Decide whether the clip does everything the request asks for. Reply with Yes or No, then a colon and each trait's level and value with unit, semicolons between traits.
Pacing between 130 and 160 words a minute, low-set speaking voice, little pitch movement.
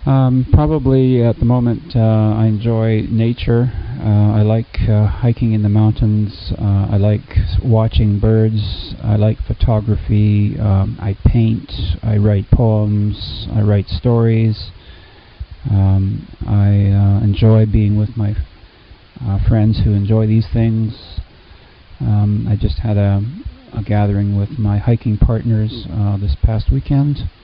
Yes: slow, 135 wpm; low, 105 Hz; narrow, 1.9 semitones